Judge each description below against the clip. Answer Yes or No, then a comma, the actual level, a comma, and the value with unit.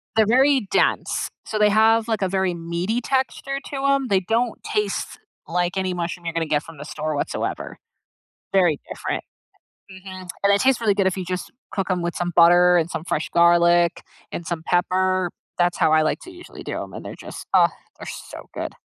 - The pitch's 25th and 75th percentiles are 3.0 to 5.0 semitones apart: Yes, average, 3.8 semitones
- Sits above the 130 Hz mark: Yes, medium, 185 Hz